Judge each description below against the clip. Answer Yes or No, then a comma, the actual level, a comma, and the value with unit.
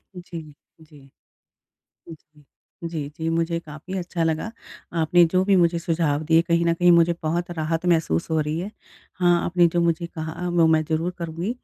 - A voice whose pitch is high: No, medium, 170 Hz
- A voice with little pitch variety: Yes, narrow, 1.5 semitones